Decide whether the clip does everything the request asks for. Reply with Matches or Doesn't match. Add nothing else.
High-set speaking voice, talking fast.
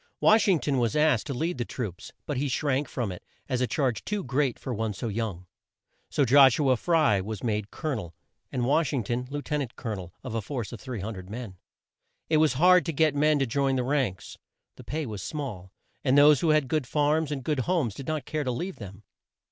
Doesn't match